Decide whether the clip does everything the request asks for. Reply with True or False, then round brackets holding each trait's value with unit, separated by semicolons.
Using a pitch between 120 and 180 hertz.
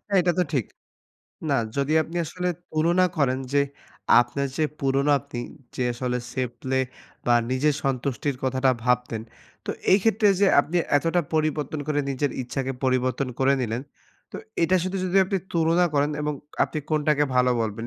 True (140 Hz)